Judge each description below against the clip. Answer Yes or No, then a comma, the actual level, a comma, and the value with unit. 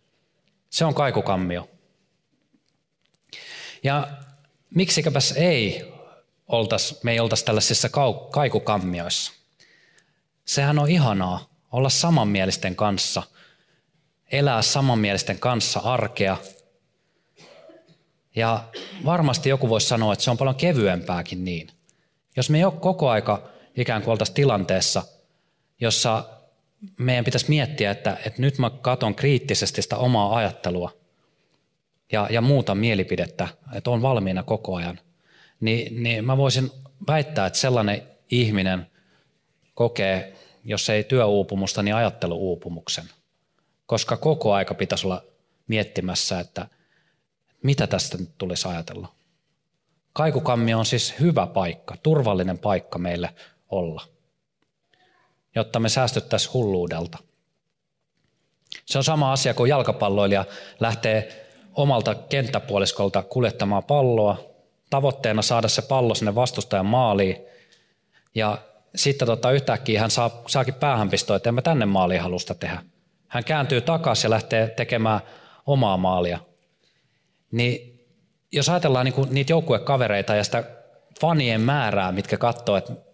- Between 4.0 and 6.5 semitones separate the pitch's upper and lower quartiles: Yes, wide, 5.5 semitones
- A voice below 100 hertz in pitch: No, low, 115 Hz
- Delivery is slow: No, average, 115 wpm